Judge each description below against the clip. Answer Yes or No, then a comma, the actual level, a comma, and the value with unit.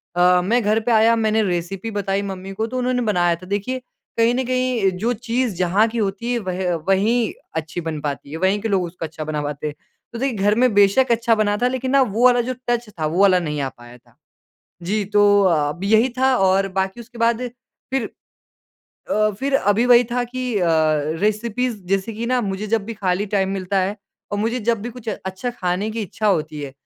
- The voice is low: No, high, 205 Hz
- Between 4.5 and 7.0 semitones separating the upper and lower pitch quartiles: No, average, 4.1 semitones